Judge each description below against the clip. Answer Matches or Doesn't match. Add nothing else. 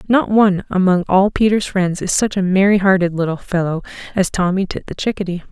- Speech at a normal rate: Matches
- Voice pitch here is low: Doesn't match